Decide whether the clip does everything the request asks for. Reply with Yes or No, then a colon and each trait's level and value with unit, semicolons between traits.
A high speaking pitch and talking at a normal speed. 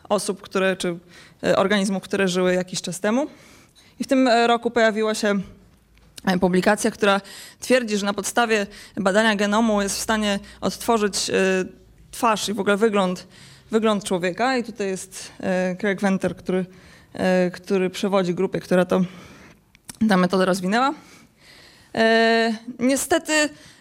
Yes: high, 200 Hz; average, 135 wpm